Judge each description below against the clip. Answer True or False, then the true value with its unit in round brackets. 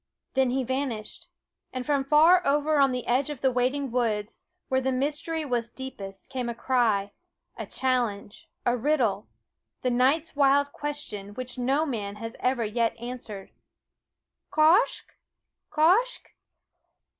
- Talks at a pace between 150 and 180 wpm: False (135 wpm)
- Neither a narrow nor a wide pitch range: True (3.5 semitones)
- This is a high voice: True (255 Hz)